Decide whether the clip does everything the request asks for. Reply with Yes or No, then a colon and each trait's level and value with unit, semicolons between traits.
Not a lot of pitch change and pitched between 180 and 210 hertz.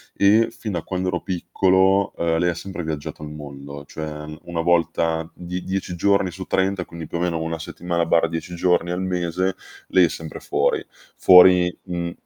No: narrow, 2.2 semitones; very low, 85 Hz